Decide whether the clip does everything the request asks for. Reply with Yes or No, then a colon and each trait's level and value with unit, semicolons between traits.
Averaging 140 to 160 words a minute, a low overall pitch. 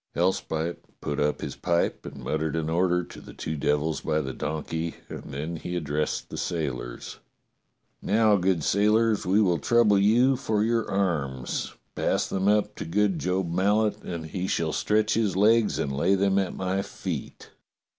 No: average, 170 wpm; very low, 90 Hz